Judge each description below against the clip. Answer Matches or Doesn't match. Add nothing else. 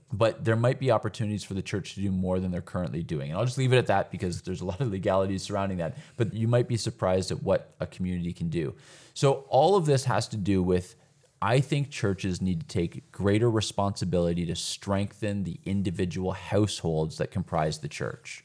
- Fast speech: Matches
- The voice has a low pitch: Matches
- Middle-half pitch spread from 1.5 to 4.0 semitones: Doesn't match